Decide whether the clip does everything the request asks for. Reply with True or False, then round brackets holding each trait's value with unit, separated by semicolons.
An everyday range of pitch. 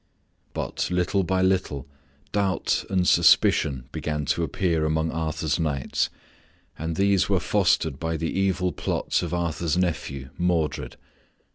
True (3.0 semitones)